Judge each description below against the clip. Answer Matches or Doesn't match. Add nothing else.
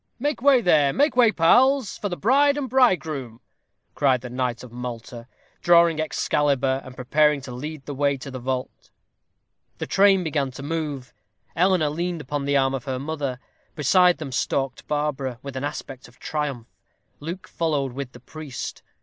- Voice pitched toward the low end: Doesn't match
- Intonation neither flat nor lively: Matches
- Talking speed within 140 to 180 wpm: Matches